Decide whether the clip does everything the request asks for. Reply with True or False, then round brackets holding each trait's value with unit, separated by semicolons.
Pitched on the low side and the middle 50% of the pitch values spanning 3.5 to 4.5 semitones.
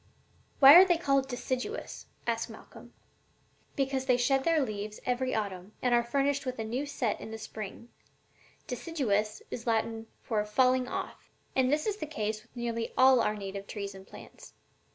False (245 Hz; 3.8 semitones)